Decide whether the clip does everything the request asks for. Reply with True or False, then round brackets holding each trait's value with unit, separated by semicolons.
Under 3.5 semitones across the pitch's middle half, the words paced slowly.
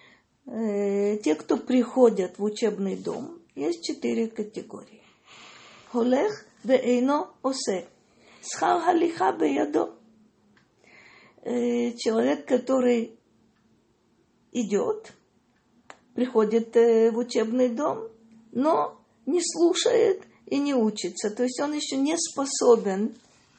False (4.3 semitones; 80 wpm)